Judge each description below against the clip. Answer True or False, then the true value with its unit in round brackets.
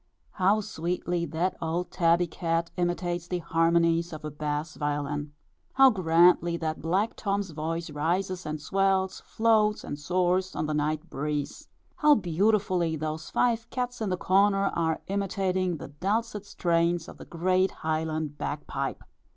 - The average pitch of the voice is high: False (175 Hz)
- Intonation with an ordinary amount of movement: True (3.3 semitones)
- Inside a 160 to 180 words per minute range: False (150 wpm)